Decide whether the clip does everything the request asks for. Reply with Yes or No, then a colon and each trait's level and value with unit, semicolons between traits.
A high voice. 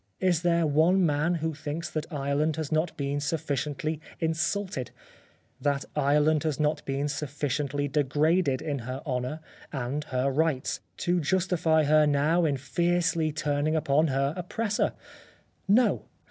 No: medium, 150 Hz